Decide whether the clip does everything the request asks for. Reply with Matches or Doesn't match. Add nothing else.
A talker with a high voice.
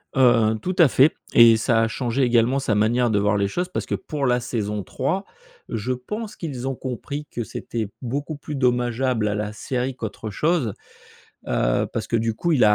Doesn't match